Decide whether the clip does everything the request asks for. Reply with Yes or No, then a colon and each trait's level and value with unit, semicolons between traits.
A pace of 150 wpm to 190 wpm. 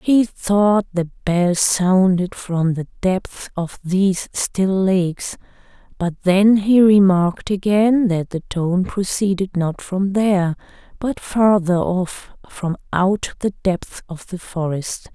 No: slow, 135 wpm